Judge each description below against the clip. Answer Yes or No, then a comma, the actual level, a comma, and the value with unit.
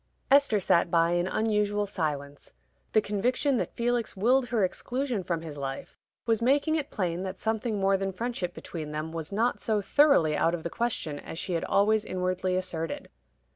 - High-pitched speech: Yes, high, 195 Hz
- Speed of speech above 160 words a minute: Yes, average, 180 wpm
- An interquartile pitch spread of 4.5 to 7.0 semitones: Yes, wide, 5.4 semitones